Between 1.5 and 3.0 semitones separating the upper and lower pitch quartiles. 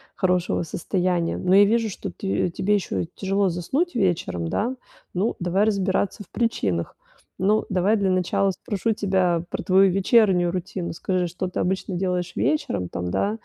Yes: narrow, 2.4 semitones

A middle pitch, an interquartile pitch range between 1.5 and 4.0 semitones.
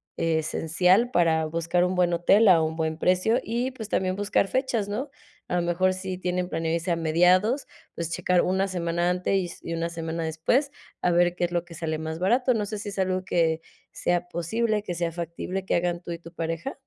Yes: medium, 175 Hz; narrow, 2.6 semitones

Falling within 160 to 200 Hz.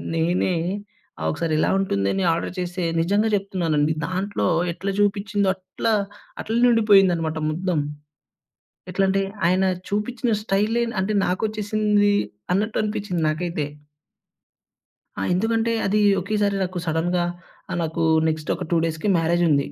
Yes: high, 190 Hz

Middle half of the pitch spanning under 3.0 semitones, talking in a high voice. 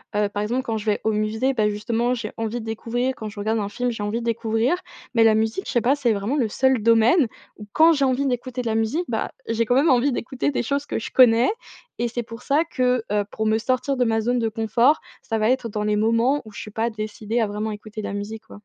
Yes: narrow, 2.6 semitones; high, 230 Hz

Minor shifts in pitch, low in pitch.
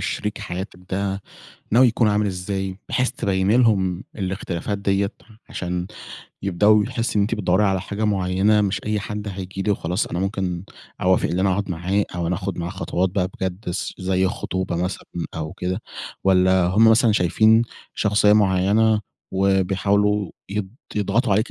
Yes: narrow, 2.2 semitones; very low, 95 Hz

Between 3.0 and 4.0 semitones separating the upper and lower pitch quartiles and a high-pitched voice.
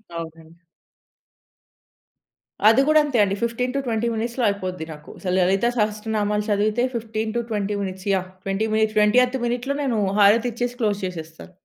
Yes: average, 3.5 semitones; high, 215 Hz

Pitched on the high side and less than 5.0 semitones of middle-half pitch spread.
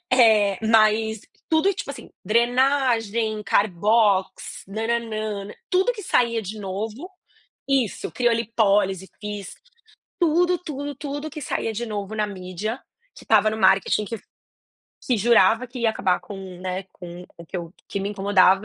Yes: high, 220 Hz; average, 3.5 semitones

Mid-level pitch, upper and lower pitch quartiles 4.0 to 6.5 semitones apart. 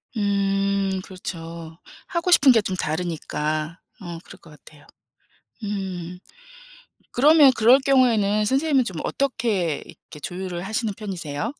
No: high, 195 Hz; wide, 5.5 semitones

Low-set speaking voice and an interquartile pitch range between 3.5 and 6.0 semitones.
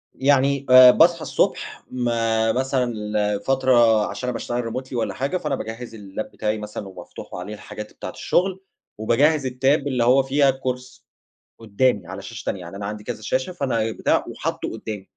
Yes: low, 120 Hz; average, 3.8 semitones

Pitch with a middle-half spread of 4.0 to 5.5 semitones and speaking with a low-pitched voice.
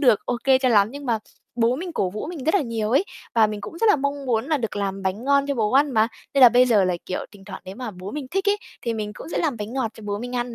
No: average, 4.8 semitones; high, 240 Hz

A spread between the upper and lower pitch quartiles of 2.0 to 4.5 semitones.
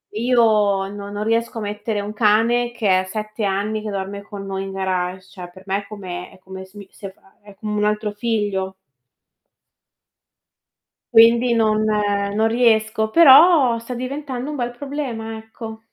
Yes: narrow, 2.6 semitones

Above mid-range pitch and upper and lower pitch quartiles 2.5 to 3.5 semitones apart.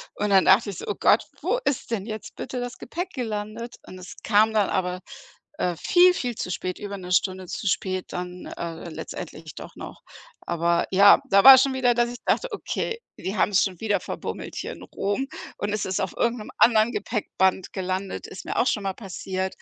No: high, 205 Hz; average, 4.1 semitones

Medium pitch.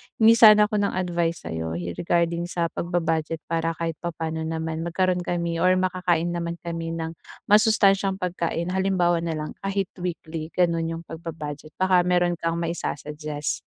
Yes: medium, 170 Hz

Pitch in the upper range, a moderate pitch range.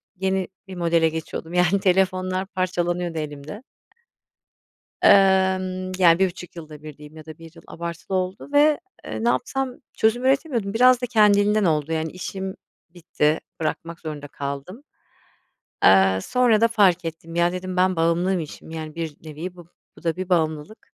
No: medium, 180 Hz; average, 3.1 semitones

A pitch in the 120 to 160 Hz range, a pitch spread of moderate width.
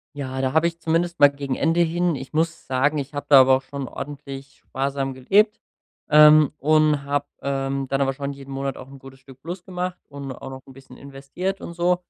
Yes: medium, 140 Hz; average, 3.0 semitones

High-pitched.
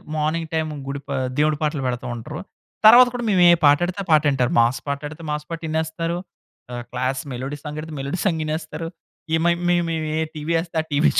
No: medium, 155 Hz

